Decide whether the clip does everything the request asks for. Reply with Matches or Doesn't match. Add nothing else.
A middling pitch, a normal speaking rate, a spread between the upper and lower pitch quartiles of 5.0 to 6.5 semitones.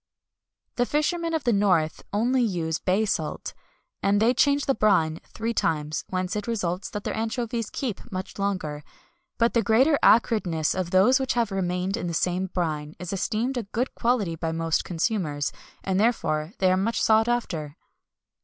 Doesn't match